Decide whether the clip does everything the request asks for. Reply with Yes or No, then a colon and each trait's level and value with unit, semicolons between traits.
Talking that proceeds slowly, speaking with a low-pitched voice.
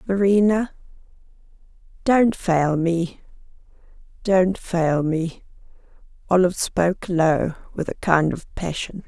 No: slow, 95 wpm; medium, 180 Hz